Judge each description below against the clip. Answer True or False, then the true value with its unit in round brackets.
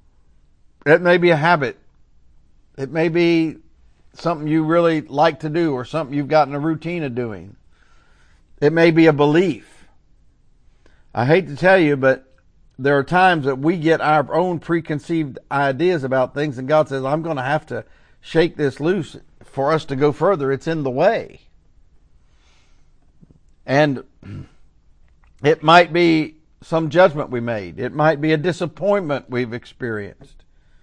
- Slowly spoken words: False (155 wpm)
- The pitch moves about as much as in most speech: True (4.8 semitones)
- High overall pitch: False (150 Hz)